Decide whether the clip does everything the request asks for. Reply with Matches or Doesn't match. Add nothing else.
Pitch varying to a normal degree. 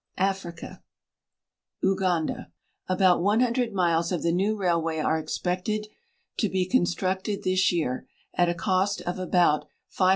Doesn't match